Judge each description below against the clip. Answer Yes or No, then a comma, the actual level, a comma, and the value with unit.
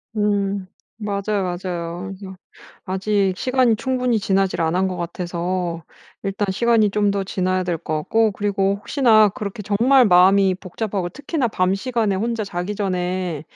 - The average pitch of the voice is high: Yes, high, 195 Hz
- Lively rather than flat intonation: No, average, 2.7 semitones